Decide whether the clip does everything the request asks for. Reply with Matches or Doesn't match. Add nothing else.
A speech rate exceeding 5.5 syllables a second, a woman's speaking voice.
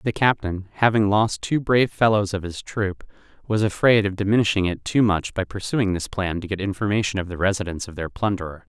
Doesn't match